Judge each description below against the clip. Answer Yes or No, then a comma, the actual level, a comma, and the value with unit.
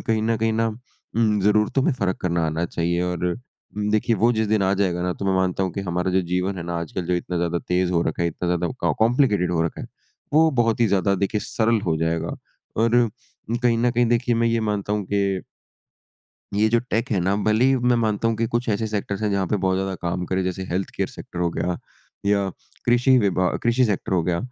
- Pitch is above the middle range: No, low, 100 Hz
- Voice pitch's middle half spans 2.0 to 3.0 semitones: No, average, 4.1 semitones